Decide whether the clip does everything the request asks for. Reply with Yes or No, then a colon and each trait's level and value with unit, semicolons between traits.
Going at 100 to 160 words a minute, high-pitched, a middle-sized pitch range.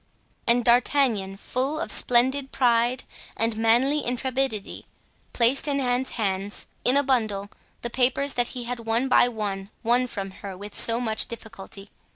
Yes: average, 155 wpm; high, 240 Hz; average, 3.1 semitones